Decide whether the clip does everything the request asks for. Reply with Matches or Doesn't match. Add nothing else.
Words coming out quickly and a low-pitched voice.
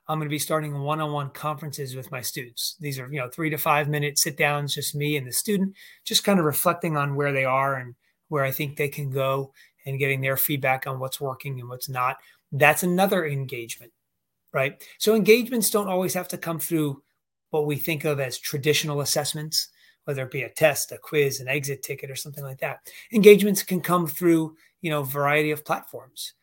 Doesn't match